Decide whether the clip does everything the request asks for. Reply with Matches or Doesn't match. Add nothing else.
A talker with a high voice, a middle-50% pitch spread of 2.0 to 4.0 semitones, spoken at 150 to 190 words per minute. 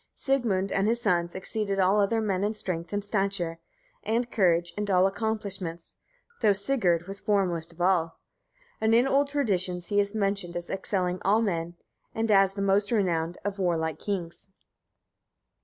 Matches